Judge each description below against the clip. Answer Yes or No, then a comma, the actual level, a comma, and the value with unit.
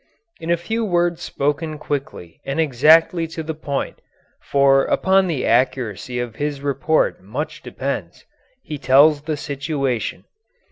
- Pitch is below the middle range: No, medium, 145 Hz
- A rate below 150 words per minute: Yes, slow, 135 wpm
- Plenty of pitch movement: No, average, 3.2 semitones